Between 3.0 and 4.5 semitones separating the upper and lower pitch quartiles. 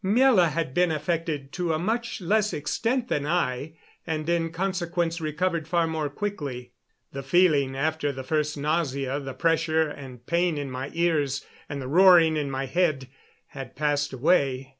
Yes: average, 3.7 semitones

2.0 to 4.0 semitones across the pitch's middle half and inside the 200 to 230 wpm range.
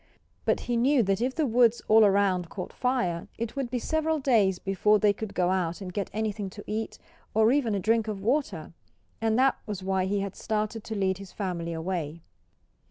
Yes: average, 3.5 semitones; fast, 205 wpm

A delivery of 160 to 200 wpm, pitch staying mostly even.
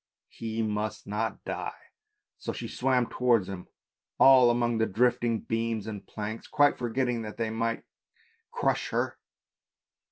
No: slow, 135 wpm; narrow, 1.8 semitones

